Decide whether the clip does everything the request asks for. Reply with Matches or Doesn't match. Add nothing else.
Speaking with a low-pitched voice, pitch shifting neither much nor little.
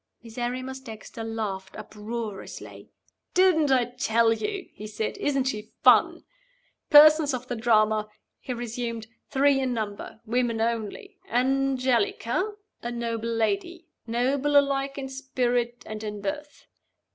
Doesn't match